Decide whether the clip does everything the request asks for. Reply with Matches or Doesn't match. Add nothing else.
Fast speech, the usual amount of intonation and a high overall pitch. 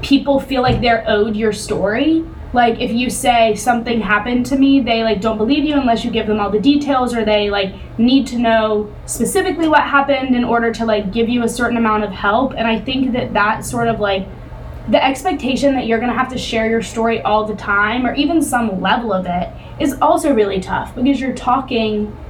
Matches